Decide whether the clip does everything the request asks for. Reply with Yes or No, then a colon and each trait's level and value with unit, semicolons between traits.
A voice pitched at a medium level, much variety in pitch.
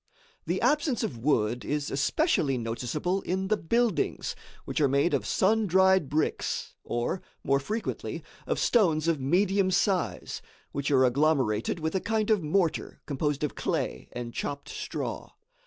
Yes: medium, 155 Hz; wide, 6.0 semitones